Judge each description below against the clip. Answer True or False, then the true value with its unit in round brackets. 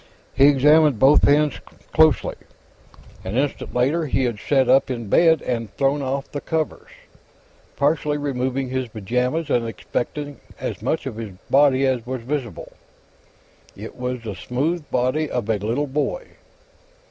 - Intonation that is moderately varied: True (3.0 semitones)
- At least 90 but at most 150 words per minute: True (145 wpm)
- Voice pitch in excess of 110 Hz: True (135 Hz)